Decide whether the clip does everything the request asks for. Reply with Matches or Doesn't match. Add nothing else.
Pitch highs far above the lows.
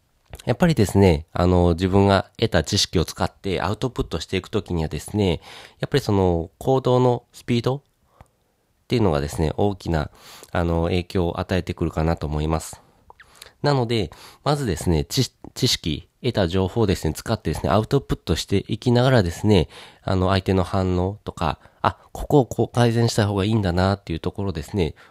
Doesn't match